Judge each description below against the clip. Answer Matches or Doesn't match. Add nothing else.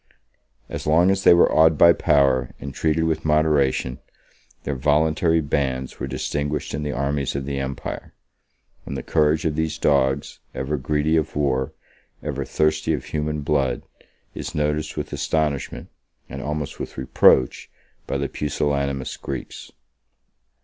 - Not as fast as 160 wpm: Matches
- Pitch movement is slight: Matches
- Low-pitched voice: Matches